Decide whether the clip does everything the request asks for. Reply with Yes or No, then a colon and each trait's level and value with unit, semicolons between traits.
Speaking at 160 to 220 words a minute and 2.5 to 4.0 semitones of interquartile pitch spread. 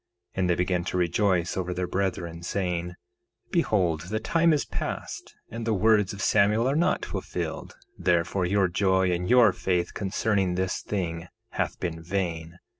Yes: average, 165 wpm; average, 2.8 semitones